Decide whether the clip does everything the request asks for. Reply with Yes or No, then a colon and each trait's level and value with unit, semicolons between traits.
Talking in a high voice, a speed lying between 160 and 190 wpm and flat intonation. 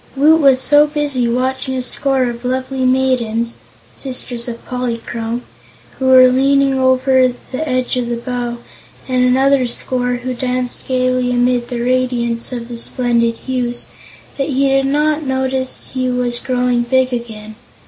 No: very high, 255 Hz; average, 150 wpm; narrow, 1.4 semitones